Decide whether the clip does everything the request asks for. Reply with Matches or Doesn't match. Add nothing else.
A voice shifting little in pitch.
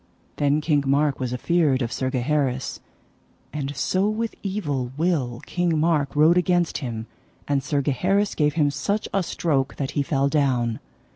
Doesn't match